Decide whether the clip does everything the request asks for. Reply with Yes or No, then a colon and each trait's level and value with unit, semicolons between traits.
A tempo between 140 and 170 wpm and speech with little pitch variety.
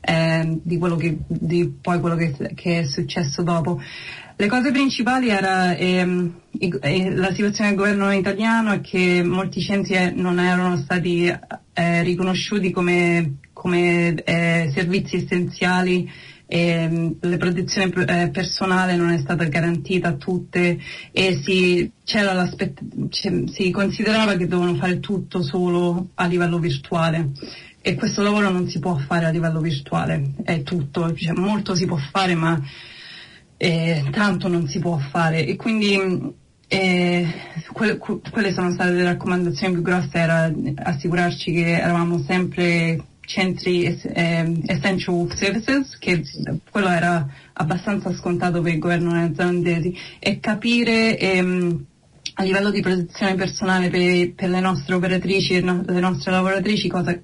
Yes: average, 145 wpm; narrow, 1.8 semitones